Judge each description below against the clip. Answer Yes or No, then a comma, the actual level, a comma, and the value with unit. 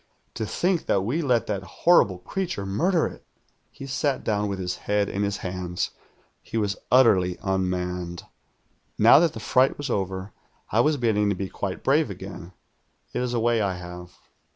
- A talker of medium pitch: No, low, 100 Hz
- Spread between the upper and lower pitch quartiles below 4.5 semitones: No, average, 5.2 semitones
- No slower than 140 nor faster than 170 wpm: No, average, 180 wpm